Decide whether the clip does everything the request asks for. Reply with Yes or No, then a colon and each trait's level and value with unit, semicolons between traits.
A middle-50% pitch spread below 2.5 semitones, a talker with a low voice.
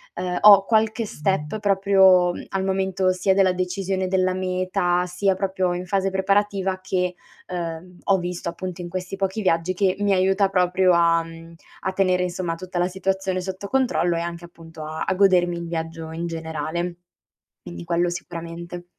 No: narrow, 1.9 semitones; medium, 185 Hz